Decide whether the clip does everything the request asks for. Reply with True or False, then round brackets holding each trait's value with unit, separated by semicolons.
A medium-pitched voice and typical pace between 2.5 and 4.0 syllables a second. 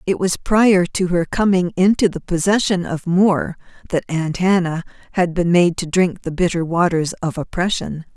False (175 Hz; 4.8 syllables/s)